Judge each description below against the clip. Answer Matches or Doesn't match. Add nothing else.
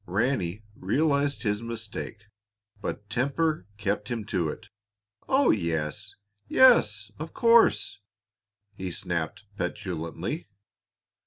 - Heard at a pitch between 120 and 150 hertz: Doesn't match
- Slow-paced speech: Matches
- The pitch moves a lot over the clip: Matches